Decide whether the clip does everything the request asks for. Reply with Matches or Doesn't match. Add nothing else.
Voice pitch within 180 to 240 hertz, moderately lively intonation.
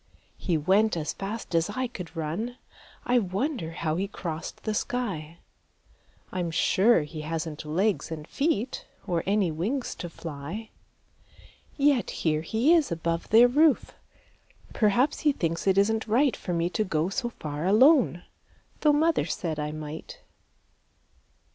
Doesn't match